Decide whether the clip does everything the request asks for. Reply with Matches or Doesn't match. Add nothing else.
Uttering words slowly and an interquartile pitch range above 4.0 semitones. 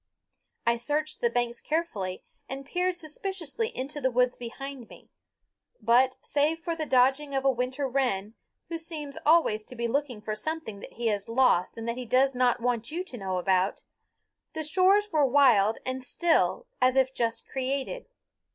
Doesn't match